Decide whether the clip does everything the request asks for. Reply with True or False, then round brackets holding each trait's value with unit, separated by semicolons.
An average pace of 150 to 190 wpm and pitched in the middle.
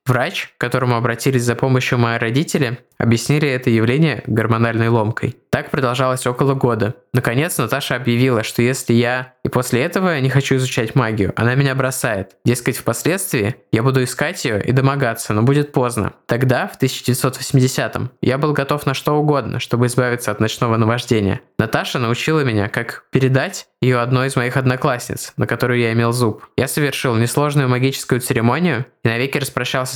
False (160 wpm; 125 Hz)